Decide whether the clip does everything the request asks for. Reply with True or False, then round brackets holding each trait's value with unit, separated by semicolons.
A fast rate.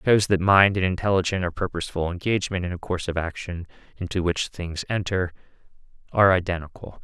False (170 wpm)